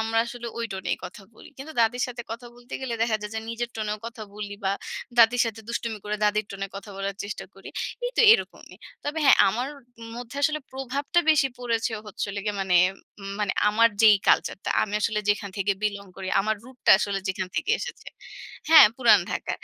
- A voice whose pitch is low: No, high, 220 Hz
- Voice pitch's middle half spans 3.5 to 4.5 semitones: No, average, 3.1 semitones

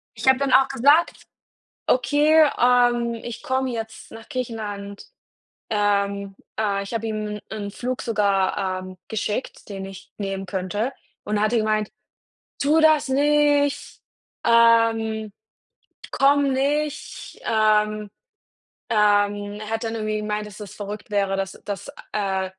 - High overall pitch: Yes, high, 215 Hz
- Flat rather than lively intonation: No, average, 3.7 semitones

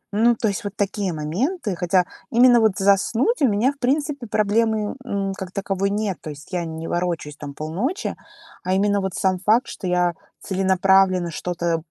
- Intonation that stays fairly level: No, average, 3.8 semitones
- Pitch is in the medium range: No, high, 195 Hz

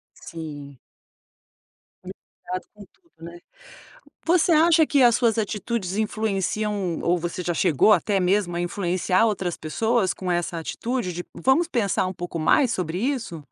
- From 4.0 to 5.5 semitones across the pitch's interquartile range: Yes, average, 4.9 semitones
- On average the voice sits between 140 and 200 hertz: Yes, high, 190 Hz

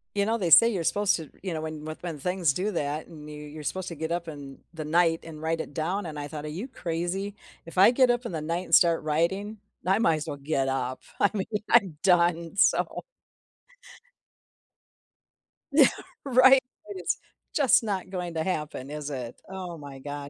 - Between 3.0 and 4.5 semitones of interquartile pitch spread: Yes, average, 4.1 semitones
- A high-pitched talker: No, medium, 165 Hz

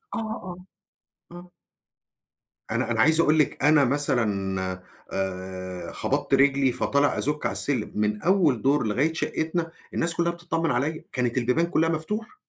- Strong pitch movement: Yes, wide, 5.7 semitones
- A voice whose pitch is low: No, medium, 145 Hz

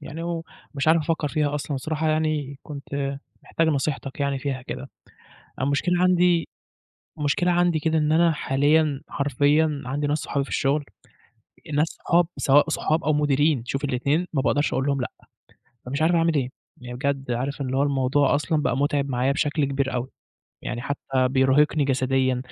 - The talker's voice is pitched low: No, medium, 145 Hz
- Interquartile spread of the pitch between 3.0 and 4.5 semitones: No, narrow, 2.5 semitones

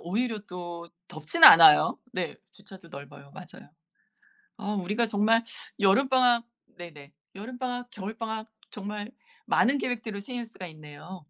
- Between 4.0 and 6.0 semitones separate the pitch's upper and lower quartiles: Yes, average, 5.2 semitones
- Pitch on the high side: Yes, high, 205 Hz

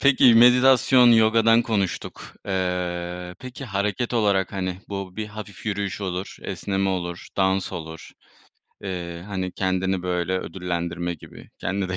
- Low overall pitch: Yes, very low, 95 Hz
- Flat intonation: No, average, 3.1 semitones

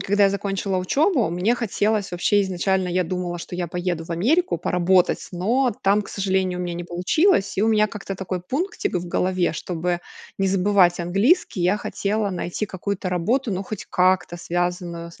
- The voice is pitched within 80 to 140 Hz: No, medium, 185 Hz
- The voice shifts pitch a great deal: No, narrow, 2.6 semitones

